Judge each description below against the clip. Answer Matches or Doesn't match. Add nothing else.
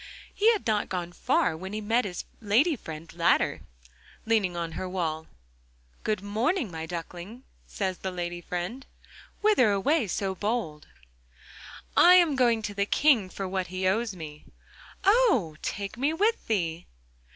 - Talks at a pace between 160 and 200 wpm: Doesn't match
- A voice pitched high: Matches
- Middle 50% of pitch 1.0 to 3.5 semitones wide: Doesn't match